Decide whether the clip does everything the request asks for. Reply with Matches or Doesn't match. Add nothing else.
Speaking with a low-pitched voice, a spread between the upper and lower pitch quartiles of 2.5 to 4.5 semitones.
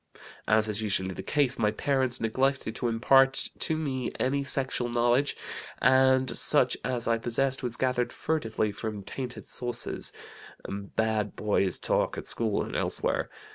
Matches